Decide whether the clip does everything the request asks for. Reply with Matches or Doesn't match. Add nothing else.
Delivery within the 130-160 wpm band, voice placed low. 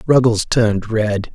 Matches